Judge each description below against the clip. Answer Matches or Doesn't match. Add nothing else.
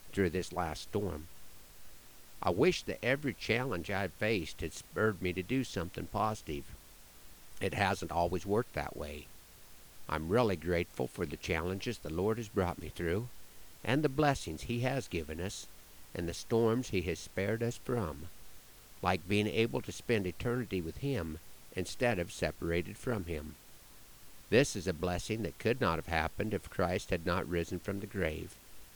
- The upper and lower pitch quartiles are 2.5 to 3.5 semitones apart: Doesn't match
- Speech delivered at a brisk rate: Doesn't match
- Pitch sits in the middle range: Doesn't match